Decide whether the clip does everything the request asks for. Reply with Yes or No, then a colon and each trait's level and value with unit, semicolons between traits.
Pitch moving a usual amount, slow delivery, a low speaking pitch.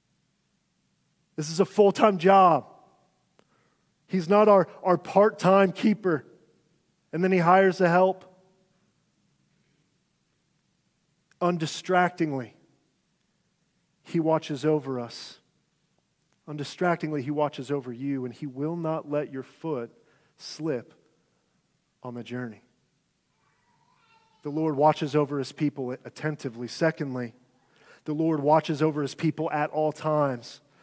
No: average, 4.1 semitones; slow, 110 wpm; medium, 155 Hz